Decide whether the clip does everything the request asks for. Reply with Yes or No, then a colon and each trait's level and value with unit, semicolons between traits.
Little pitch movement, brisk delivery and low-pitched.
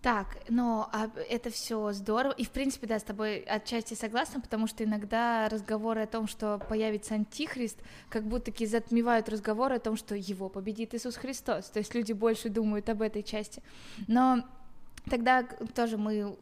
No: narrow, 1.8 semitones; fast, 170 wpm; high, 225 Hz